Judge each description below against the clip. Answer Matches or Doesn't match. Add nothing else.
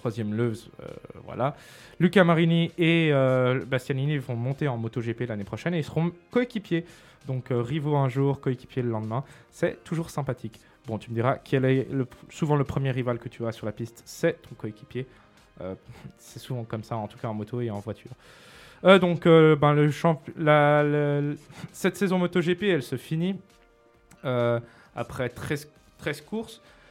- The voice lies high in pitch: Doesn't match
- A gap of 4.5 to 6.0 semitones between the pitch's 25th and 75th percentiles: Matches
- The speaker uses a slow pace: Doesn't match